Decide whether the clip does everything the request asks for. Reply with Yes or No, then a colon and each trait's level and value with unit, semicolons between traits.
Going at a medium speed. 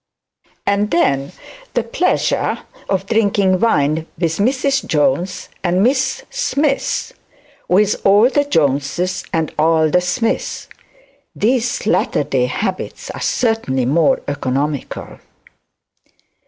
No: slow, 105 wpm